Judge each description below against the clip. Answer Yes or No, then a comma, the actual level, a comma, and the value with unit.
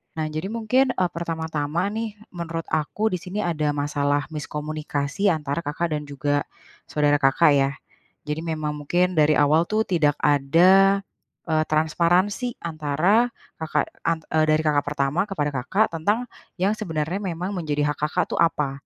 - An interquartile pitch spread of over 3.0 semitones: Yes, average, 3.6 semitones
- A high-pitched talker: No, medium, 155 Hz